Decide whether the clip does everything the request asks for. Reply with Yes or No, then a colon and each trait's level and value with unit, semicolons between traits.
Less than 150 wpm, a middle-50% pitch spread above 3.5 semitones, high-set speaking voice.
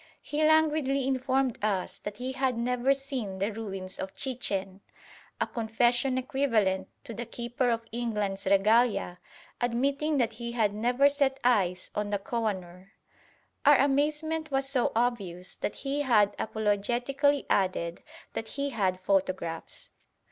Yes: average, 140 wpm; average, 5.1 semitones; high, 235 Hz